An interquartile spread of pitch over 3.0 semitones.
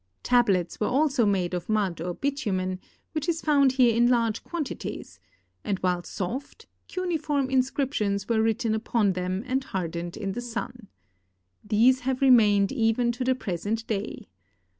Yes: average, 4.8 semitones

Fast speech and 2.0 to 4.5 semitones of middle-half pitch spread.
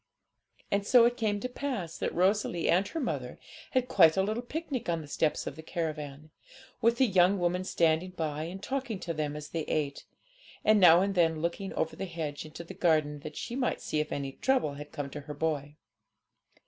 No: fast, 210 wpm; average, 5.1 semitones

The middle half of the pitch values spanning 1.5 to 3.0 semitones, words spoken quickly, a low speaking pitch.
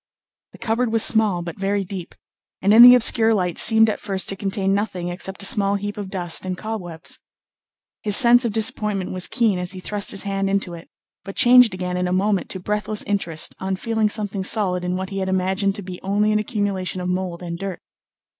No: narrow, 2.4 semitones; fast, 215 wpm; high, 195 Hz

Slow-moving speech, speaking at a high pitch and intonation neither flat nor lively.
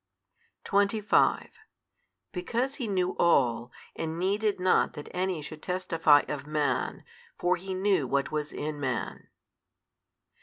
No: slow, 120 wpm; medium, 175 Hz; average, 4.5 semitones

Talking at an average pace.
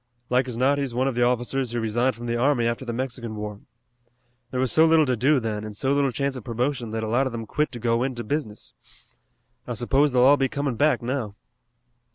No: fast, 235 wpm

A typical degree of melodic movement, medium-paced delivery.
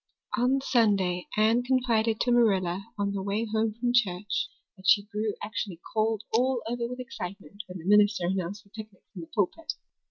Yes: average, 3.3 semitones; average, 180 wpm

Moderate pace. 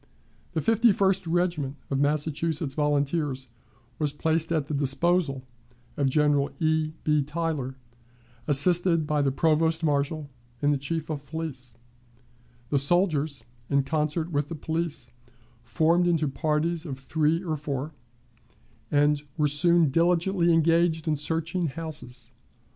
No: slow, 130 wpm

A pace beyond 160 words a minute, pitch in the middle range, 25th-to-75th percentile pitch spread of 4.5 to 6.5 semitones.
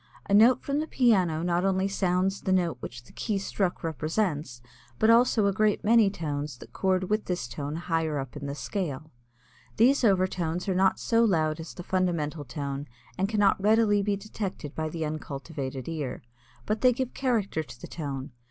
Yes: average, 180 wpm; medium, 180 Hz; average, 5.1 semitones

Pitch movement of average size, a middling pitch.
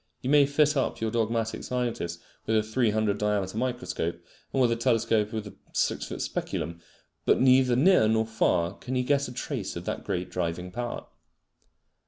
No: average, 3.9 semitones; low, 110 Hz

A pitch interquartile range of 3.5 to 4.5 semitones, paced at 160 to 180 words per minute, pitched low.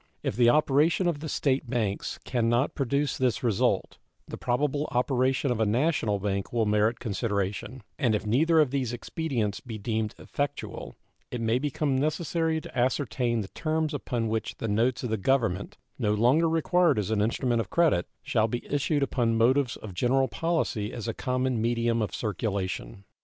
Yes: average, 4.2 semitones; average, 175 wpm; low, 120 Hz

